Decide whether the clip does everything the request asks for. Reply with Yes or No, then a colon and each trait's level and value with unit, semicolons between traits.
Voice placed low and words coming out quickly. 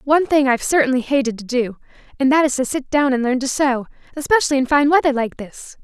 No: very high, 270 Hz; fast, 235 wpm